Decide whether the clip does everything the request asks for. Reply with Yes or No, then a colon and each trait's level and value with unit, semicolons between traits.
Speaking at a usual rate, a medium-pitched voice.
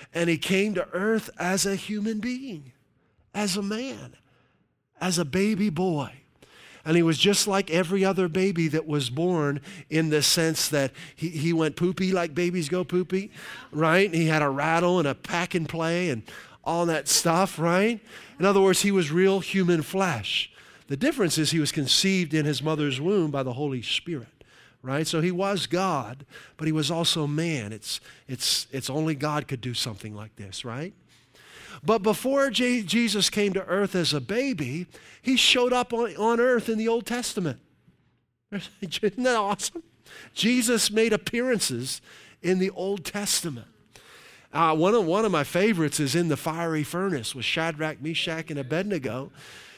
Yes: average, 175 wpm; medium, 170 Hz